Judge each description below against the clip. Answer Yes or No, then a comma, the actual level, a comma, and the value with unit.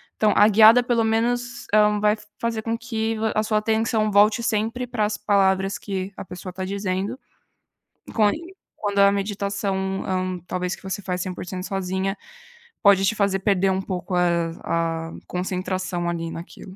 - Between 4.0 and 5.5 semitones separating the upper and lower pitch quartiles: No, average, 2.7 semitones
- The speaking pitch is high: Yes, high, 200 Hz